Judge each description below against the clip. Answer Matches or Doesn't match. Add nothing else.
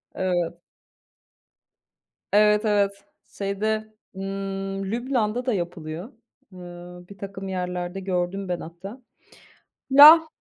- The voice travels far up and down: Doesn't match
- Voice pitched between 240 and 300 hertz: Doesn't match